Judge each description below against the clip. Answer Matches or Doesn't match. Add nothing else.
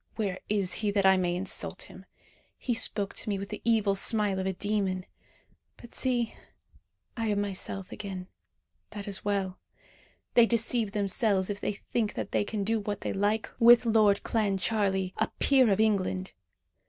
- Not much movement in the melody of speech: Matches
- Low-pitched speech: Doesn't match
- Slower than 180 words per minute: Matches